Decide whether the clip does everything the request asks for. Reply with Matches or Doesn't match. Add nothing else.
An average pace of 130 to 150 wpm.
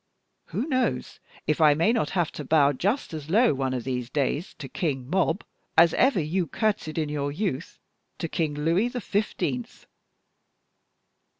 Doesn't match